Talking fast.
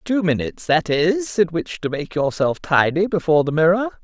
No: average, 195 wpm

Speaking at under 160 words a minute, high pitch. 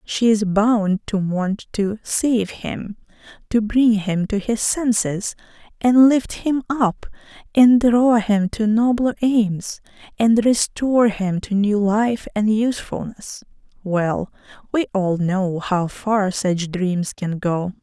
Yes: average, 140 wpm; high, 210 Hz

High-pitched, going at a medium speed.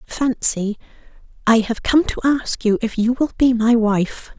Yes: high, 235 Hz; average, 180 wpm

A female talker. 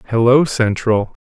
No: male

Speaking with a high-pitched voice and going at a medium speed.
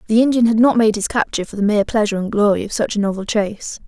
No: high, 215 Hz; fast, 280 wpm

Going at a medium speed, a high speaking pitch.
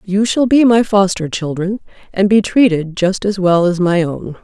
Yes: average, 190 wpm; high, 195 Hz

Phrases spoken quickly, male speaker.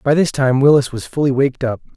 Yes: fast, 245 wpm; male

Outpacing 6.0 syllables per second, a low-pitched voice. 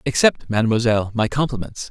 Yes: 6.3 syllables/s; low, 120 Hz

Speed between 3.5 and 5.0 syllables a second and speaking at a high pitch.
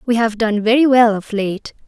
Yes: 4.8 syllables/s; high, 225 Hz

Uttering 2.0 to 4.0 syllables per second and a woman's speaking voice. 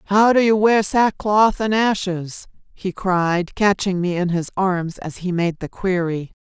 Yes: 3.9 syllables/s; female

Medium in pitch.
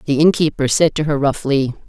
Yes: medium, 145 Hz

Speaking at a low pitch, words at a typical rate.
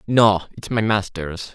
Yes: low, 100 Hz; average, 155 wpm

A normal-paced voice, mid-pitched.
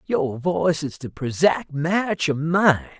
Yes: average, 160 wpm; medium, 160 Hz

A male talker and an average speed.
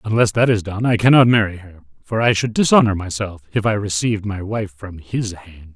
No: male; fast, 220 wpm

